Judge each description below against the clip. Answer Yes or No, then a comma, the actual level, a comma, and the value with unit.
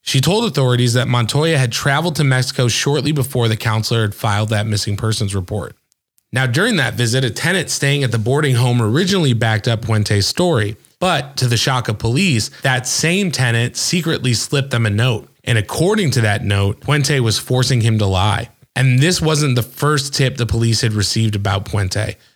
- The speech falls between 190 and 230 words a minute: Yes, average, 195 wpm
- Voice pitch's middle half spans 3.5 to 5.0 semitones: Yes, average, 4.1 semitones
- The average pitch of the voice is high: No, low, 125 Hz